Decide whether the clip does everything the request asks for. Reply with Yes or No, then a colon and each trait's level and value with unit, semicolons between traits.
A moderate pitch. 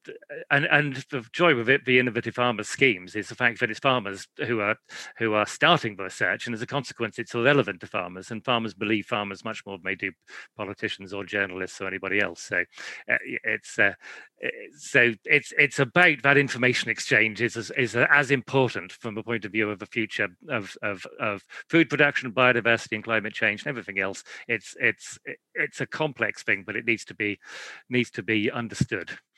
No: low, 115 Hz